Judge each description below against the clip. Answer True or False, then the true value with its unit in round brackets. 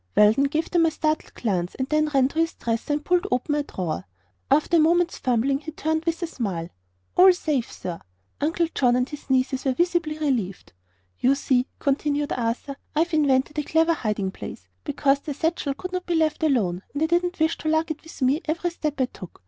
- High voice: True (295 Hz)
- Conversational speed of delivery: False (210 wpm)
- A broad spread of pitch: False (4.0 semitones)